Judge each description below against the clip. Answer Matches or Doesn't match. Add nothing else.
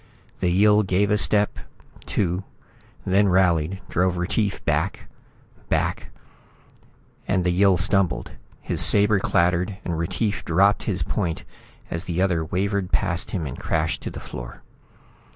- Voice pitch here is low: Matches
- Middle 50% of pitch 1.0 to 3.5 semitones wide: Matches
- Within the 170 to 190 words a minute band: Doesn't match